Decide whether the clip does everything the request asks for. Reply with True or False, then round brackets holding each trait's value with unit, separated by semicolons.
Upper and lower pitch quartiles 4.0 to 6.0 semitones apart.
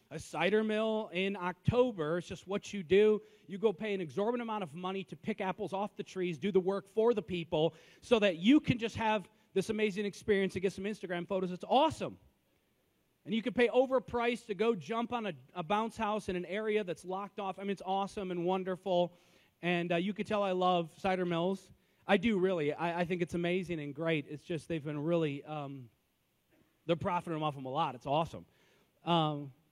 False (3.6 semitones)